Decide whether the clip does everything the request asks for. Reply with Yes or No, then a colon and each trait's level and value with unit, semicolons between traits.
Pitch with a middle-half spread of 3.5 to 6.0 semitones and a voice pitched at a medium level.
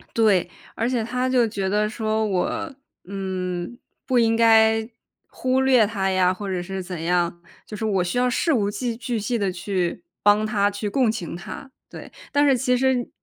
No: average, 4.2 semitones; high, 215 Hz